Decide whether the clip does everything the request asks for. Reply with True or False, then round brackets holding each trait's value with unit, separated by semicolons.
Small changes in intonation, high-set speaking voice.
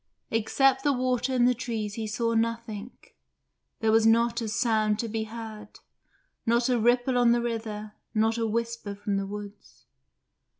True (1.8 semitones; 230 Hz)